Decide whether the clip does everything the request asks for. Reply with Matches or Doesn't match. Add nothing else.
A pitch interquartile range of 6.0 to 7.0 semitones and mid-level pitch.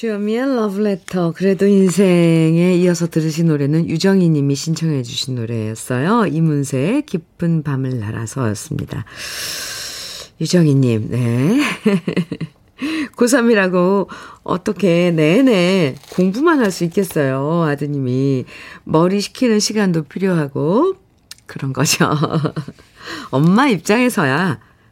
Doesn't match